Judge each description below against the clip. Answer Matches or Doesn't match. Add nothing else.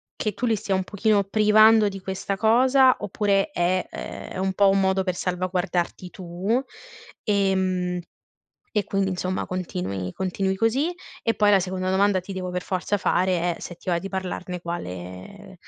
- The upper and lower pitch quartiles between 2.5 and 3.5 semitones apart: Doesn't match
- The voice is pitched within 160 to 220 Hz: Matches